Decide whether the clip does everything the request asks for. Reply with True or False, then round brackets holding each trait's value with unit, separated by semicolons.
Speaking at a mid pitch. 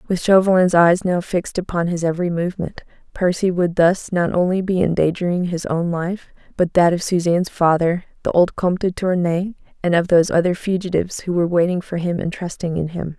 True (175 Hz)